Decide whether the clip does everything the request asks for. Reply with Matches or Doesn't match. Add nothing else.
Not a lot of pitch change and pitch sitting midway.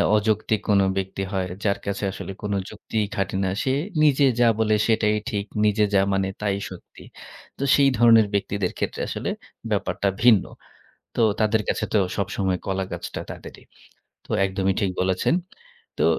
Doesn't match